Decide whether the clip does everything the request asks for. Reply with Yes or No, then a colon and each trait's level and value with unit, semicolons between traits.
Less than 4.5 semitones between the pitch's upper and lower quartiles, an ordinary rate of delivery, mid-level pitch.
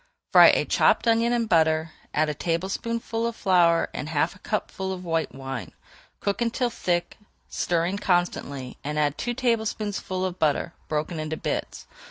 No: wide, 5.4 semitones; average, 160 wpm; medium, 175 Hz